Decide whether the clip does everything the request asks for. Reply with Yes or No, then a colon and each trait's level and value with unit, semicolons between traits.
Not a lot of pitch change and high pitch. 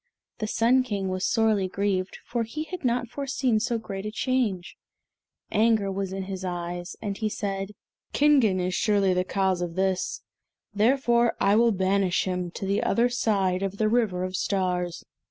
No: average, 3.7 semitones; high, 200 Hz